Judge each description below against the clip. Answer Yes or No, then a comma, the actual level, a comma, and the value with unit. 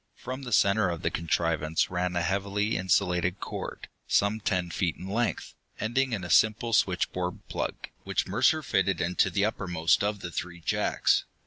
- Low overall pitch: Yes, very low, 95 Hz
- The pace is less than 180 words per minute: Yes, average, 165 wpm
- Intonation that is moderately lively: Yes, average, 3.2 semitones